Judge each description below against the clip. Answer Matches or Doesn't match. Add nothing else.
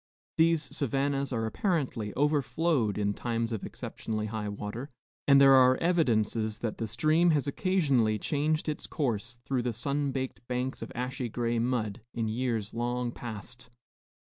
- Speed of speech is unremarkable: Matches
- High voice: Doesn't match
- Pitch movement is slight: Doesn't match